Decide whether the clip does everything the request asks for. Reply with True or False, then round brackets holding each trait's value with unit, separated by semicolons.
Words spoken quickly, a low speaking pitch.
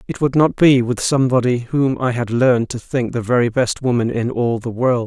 True (235 wpm; 125 Hz)